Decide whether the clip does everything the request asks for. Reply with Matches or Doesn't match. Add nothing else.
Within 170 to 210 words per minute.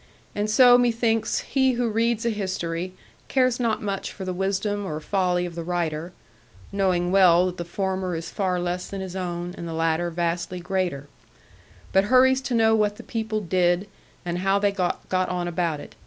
Matches